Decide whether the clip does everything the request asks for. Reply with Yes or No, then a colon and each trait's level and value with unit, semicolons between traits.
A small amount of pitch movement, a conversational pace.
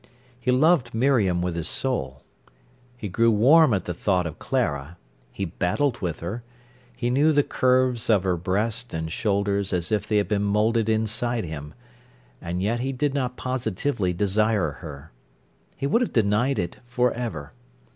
No: wide, 5.6 semitones; average, 165 wpm